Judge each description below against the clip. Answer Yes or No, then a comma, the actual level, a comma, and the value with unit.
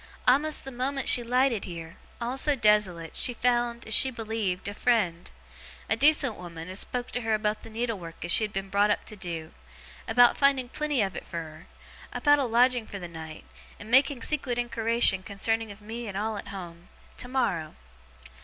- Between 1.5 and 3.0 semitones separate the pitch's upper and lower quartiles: No, average, 4.5 semitones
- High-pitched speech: Yes, high, 225 Hz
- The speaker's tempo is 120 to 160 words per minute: No, average, 200 wpm